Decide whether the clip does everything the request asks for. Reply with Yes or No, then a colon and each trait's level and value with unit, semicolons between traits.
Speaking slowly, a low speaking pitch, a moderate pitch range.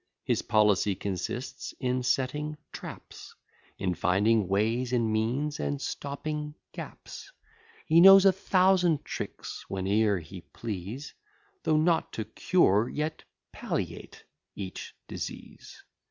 No: slow, 110 wpm; low, 125 Hz; wide, 6.7 semitones